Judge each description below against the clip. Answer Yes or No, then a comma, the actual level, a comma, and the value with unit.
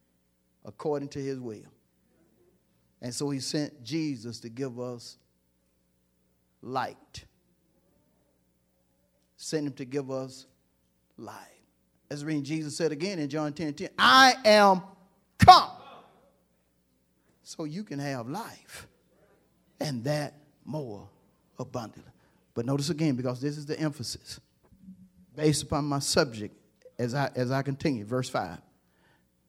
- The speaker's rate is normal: No, slow, 120 wpm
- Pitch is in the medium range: No, low, 130 Hz